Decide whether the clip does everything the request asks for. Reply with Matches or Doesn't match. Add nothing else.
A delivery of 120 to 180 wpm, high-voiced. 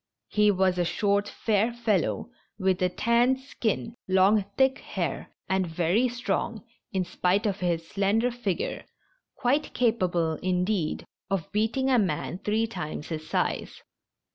Matches